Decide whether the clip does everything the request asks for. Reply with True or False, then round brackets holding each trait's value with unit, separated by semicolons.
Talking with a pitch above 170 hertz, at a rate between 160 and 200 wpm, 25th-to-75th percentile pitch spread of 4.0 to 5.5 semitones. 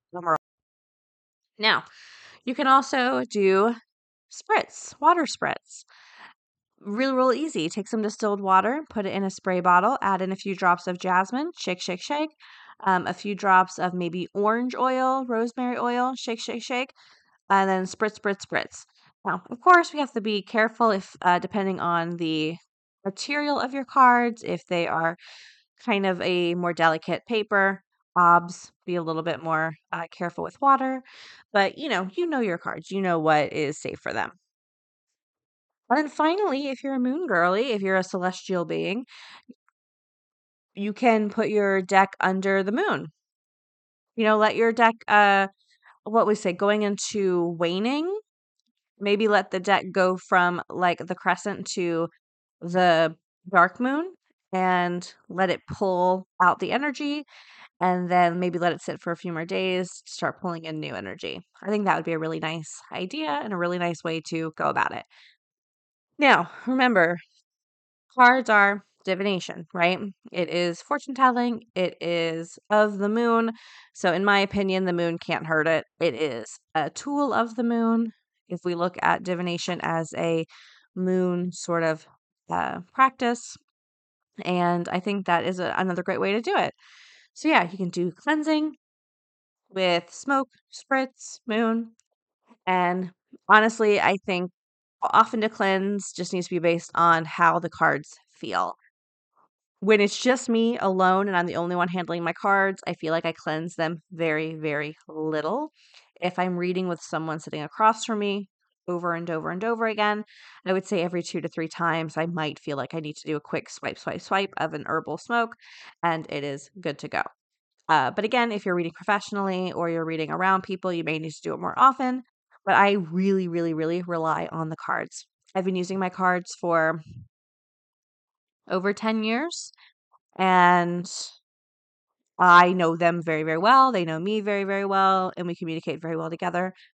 True (185 Hz; 170 wpm; 4.4 semitones)